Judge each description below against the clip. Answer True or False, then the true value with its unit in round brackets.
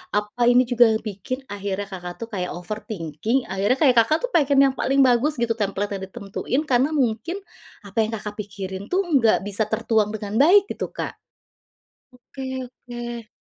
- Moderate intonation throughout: True (3.8 semitones)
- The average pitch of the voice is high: True (220 Hz)